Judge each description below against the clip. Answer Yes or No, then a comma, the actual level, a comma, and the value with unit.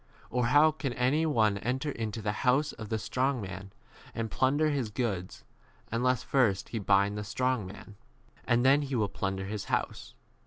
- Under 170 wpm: No, average, 185 wpm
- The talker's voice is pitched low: Yes, low, 115 Hz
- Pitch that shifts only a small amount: No, average, 4.2 semitones